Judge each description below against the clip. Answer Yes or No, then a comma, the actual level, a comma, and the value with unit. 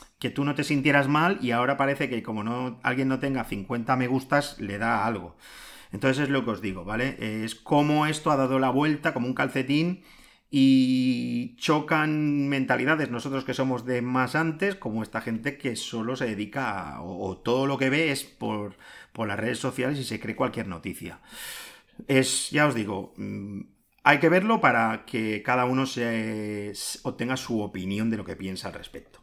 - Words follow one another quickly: Yes, fast, 195 wpm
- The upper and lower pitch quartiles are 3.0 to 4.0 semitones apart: No, average, 4.4 semitones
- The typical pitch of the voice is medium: No, low, 130 Hz